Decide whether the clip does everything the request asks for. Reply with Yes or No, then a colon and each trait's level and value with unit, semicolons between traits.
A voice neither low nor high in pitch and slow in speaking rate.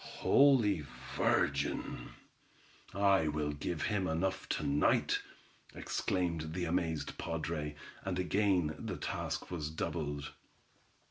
No: very low, 85 Hz; slow, 105 wpm